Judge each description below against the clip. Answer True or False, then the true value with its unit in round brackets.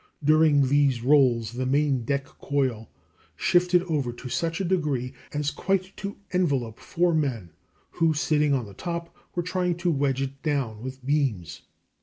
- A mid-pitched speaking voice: True (145 Hz)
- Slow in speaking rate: False (160 wpm)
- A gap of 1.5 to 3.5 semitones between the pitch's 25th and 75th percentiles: False (4.4 semitones)